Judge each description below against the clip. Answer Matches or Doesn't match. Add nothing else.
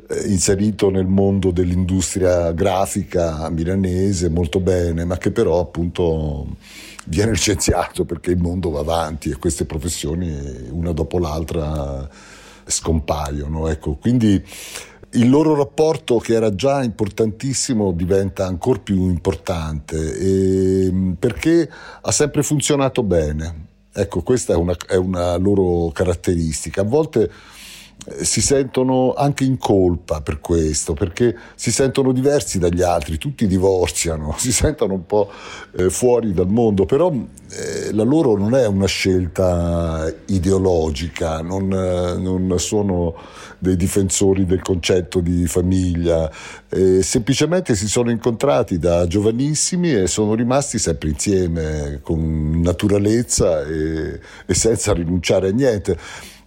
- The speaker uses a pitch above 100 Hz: Doesn't match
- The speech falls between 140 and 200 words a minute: Doesn't match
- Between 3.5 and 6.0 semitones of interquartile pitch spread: Matches